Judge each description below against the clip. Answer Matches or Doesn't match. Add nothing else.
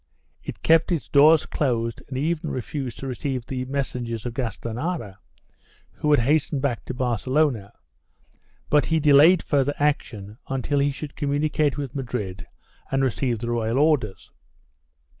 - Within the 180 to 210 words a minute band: Doesn't match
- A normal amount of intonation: Matches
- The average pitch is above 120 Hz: Matches